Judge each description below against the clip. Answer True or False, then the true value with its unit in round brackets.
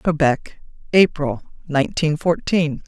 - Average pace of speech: False (85 wpm)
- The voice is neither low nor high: True (155 Hz)